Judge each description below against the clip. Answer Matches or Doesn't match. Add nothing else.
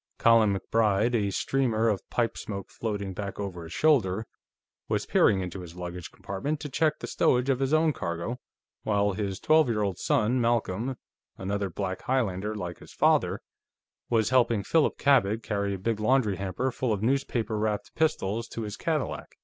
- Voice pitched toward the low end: Matches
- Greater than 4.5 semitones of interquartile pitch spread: Doesn't match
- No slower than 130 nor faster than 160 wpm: Doesn't match